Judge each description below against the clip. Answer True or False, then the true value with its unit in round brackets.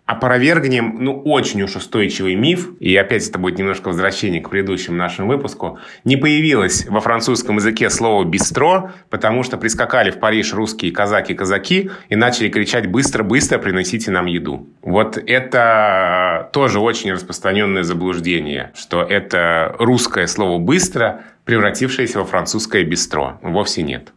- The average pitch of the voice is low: True (110 Hz)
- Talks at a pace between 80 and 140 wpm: True (135 wpm)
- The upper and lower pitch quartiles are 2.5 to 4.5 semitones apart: False (5.2 semitones)